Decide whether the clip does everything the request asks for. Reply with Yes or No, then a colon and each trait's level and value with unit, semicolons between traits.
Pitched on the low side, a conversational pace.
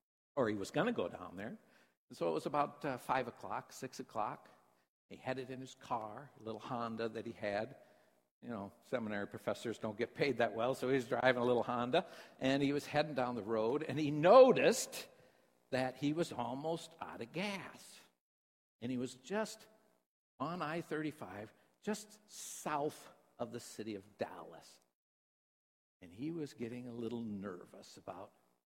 Yes: low, 125 Hz; average, 175 wpm